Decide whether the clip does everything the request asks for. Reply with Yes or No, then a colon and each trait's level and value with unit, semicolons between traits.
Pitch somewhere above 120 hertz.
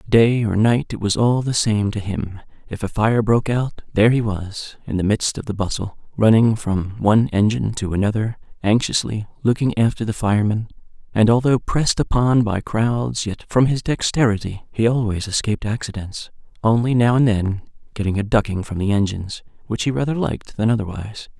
No: low, 110 Hz